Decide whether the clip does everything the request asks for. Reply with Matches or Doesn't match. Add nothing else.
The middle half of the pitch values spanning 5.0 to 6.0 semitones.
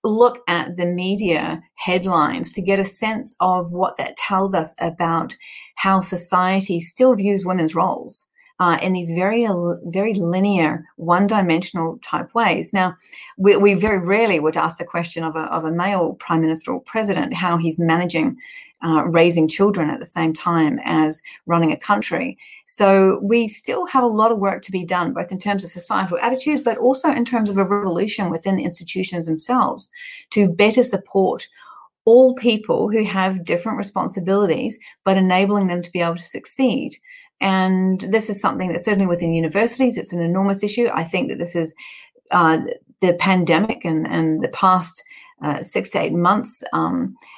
Doesn't match